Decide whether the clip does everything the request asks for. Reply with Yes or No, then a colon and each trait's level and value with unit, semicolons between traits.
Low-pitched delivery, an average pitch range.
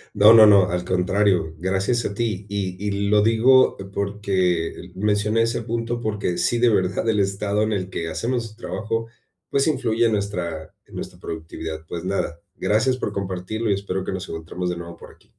Yes: low, 100 Hz; average, 3.6 semitones